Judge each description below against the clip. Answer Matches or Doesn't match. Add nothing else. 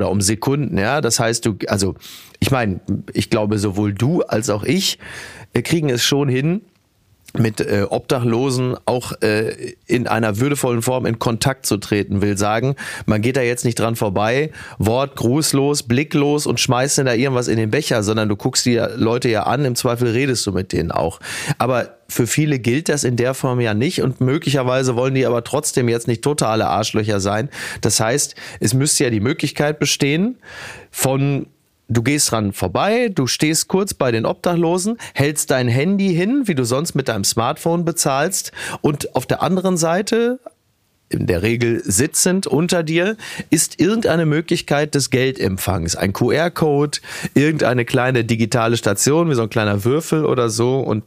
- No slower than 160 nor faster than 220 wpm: Matches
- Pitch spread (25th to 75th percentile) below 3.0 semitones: Doesn't match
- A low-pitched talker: Matches